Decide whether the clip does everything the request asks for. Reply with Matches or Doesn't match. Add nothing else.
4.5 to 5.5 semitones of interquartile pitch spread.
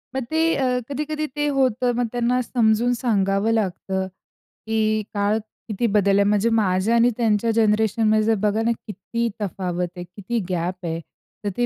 Doesn't match